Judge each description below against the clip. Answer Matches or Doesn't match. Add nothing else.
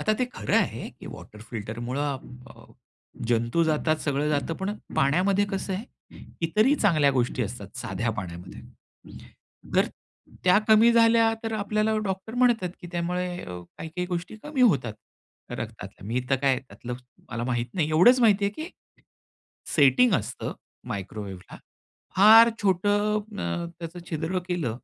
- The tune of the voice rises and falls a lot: Matches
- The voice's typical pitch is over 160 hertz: Matches